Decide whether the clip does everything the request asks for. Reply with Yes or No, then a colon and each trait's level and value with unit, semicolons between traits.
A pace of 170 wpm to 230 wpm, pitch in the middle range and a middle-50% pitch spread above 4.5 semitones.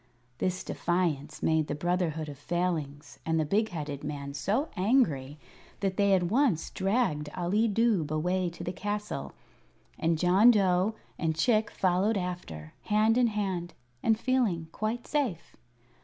No: average, 145 wpm; medium, 180 Hz; average, 5.0 semitones